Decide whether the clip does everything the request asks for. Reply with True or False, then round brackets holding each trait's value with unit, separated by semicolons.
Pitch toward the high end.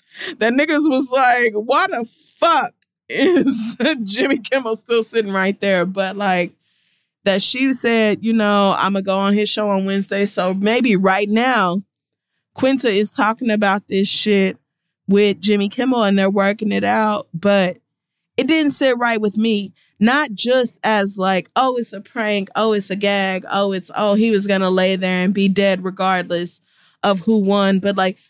True (205 Hz)